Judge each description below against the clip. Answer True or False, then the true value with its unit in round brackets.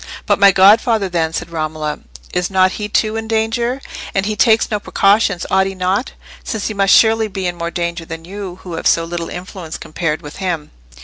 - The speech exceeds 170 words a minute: True (200 wpm)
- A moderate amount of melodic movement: True (3.8 semitones)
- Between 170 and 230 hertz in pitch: True (190 Hz)